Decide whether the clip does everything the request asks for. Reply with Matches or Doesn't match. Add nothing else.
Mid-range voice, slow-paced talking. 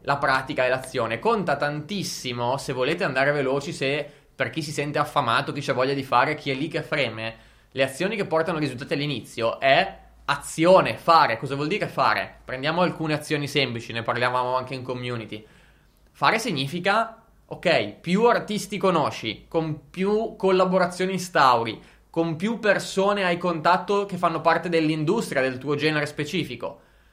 Doesn't match